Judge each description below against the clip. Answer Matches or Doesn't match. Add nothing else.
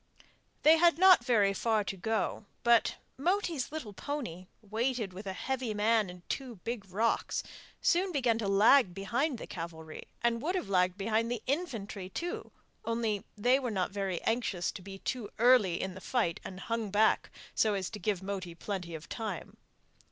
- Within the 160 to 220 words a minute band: Matches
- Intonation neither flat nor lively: Matches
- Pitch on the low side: Doesn't match